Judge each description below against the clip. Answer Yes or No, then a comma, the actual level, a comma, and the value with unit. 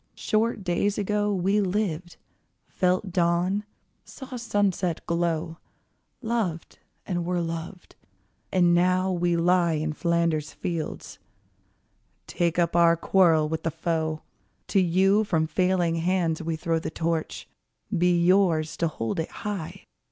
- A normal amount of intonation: No, narrow, 2.3 semitones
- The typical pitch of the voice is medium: Yes, medium, 175 Hz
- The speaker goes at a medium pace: No, slow, 130 wpm